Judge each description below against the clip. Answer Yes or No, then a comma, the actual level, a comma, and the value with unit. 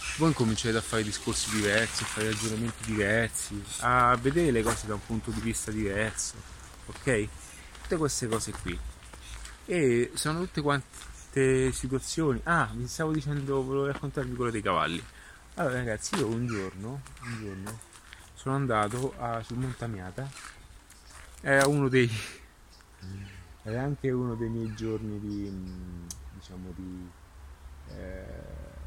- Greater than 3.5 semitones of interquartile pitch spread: Yes, average, 5.3 semitones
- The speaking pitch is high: No, low, 110 Hz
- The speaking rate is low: No, average, 135 wpm